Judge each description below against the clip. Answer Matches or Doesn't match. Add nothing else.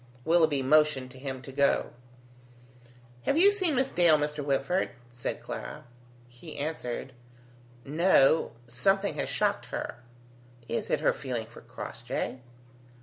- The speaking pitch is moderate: Matches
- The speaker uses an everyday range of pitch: Matches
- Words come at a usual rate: Doesn't match